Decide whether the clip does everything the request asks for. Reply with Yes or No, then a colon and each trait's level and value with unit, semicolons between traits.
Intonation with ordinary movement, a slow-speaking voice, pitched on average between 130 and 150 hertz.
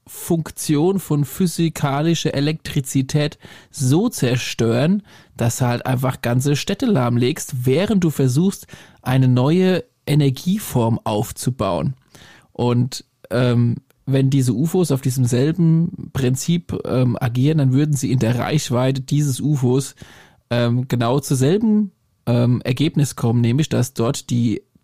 Yes: average, 3.8 semitones; slow, 120 wpm; low, 135 Hz